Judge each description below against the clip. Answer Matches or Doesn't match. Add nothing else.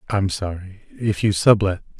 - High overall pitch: Doesn't match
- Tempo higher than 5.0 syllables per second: Doesn't match